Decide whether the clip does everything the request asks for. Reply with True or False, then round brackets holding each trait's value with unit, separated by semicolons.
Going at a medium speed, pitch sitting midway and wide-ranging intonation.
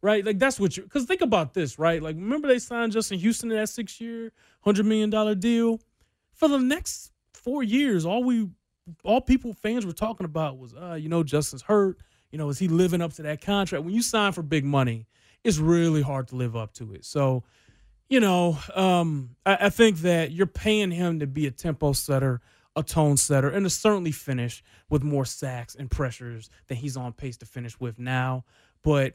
False (210 wpm; 165 Hz; 8.1 semitones)